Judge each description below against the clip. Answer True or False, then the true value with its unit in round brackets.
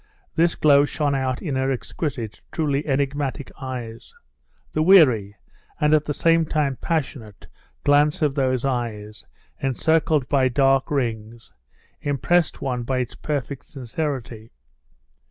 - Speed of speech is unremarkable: False (125 wpm)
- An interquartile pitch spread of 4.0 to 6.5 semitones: False (3.2 semitones)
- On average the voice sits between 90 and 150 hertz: True (135 Hz)